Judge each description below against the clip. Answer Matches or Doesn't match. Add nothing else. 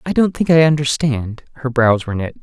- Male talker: Matches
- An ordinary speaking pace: Doesn't match